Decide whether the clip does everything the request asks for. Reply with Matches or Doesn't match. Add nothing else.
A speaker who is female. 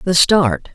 Matches